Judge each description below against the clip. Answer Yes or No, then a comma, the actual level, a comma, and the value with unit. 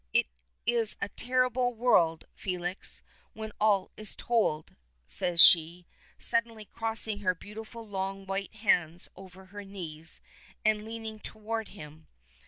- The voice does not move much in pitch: No, average, 3.6 semitones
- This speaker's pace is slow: Yes, slow, 125 wpm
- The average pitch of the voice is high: Yes, high, 205 Hz